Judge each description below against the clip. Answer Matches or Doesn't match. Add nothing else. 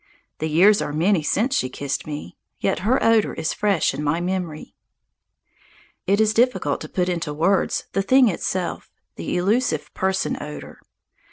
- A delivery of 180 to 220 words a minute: Doesn't match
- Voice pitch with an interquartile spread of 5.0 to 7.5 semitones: Matches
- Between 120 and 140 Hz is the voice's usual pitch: Doesn't match